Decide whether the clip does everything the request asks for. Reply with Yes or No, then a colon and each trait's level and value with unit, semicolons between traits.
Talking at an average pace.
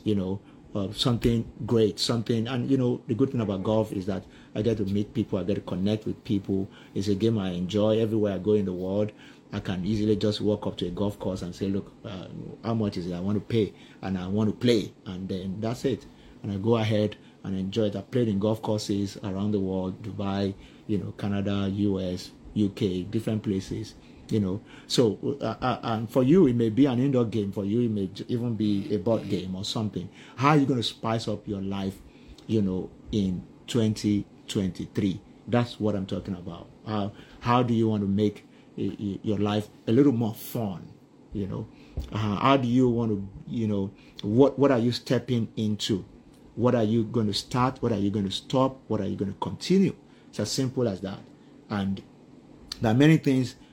No: fast, 220 wpm